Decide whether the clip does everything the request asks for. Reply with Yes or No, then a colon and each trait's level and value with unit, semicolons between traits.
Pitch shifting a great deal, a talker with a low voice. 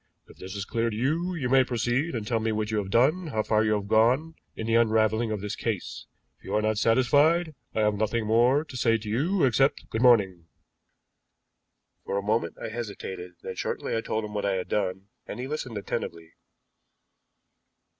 No: average, 3.4 semitones; low, 110 Hz